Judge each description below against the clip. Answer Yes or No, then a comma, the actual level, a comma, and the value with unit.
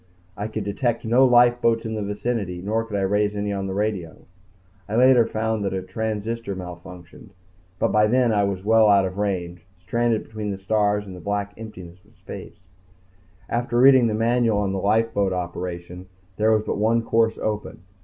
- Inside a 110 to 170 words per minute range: No, average, 185 wpm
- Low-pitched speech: Yes, low, 105 Hz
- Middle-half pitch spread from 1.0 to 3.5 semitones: Yes, average, 2.8 semitones